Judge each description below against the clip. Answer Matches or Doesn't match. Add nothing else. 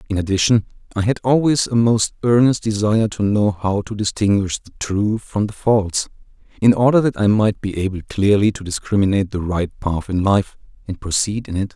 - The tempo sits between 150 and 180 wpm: Doesn't match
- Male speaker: Matches